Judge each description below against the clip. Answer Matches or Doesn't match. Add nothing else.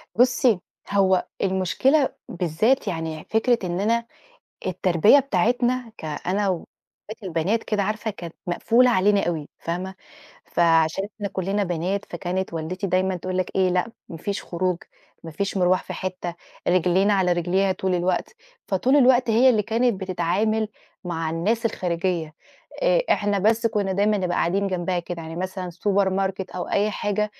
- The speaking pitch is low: Doesn't match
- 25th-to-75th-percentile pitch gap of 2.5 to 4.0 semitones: Matches